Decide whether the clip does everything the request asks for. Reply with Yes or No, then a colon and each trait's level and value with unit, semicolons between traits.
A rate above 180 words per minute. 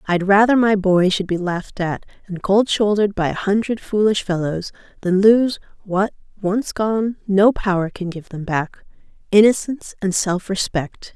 No: average, 160 wpm